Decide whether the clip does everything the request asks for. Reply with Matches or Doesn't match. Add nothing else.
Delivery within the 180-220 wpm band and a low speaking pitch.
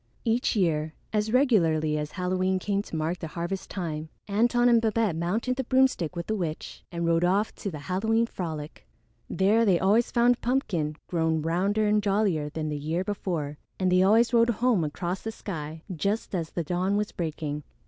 Doesn't match